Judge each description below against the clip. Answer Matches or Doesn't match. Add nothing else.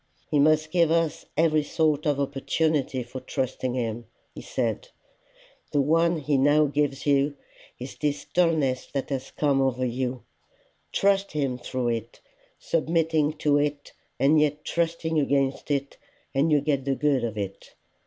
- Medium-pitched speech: Matches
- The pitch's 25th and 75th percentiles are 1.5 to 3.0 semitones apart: Matches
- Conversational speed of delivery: Matches